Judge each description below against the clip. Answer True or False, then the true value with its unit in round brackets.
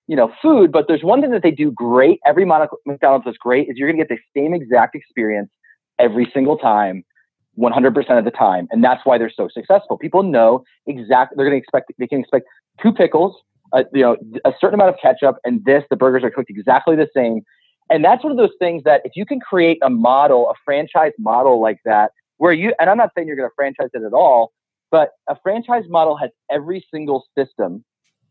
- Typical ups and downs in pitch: False (5.9 semitones)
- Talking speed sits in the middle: False (225 wpm)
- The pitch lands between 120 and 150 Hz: True (140 Hz)